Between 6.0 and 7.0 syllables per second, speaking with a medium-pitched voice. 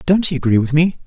Yes: 6.7 syllables/s; medium, 155 Hz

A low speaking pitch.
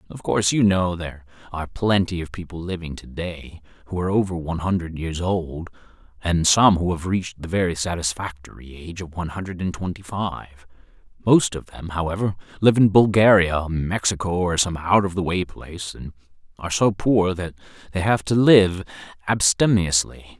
Yes: very low, 90 Hz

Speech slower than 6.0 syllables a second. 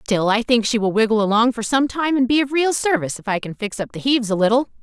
No: 6.6 syllables/s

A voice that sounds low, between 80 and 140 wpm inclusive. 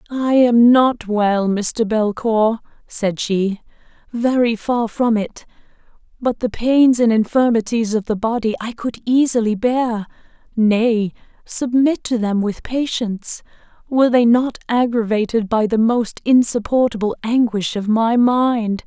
No: high, 230 Hz; slow, 135 wpm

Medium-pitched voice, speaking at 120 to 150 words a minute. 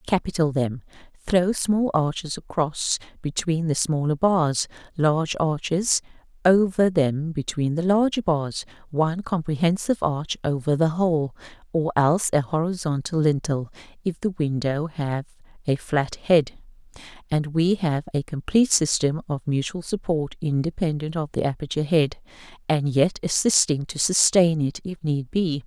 Yes: medium, 160 Hz; average, 140 wpm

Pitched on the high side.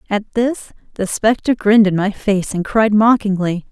Yes: high, 210 Hz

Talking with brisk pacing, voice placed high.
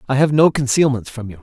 No: fast, 250 wpm; low, 130 Hz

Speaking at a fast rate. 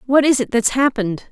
Yes: fast, 230 wpm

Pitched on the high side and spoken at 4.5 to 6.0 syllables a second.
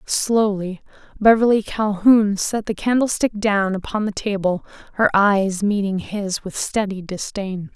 No: high, 205 Hz; 4.1 syllables/s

